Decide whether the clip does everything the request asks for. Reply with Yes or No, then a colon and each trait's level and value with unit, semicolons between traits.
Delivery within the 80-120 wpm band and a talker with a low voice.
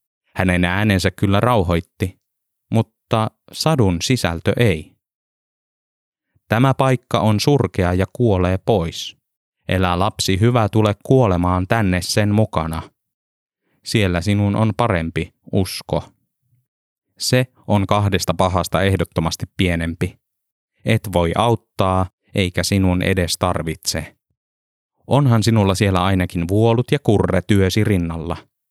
Yes: average, 105 wpm; low, 100 Hz